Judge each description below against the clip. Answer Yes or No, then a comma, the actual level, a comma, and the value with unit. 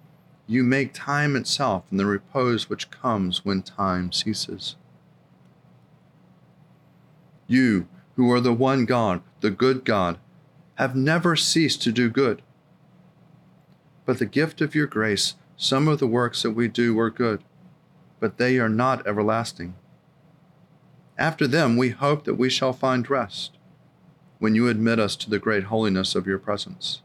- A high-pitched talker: No, low, 130 Hz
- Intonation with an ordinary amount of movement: No, wide, 5.9 semitones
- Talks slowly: No, average, 150 wpm